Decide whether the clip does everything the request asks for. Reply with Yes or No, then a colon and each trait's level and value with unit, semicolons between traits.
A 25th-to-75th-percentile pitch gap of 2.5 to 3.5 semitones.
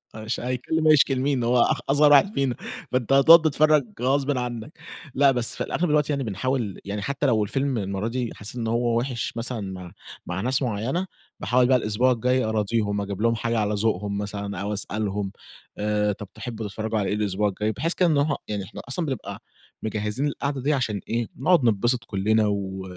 No: average, 4.4 semitones